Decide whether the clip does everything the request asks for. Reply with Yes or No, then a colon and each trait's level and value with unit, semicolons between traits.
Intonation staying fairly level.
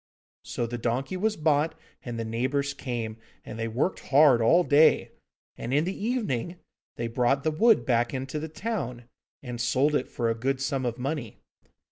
No: average, 4.6 semitones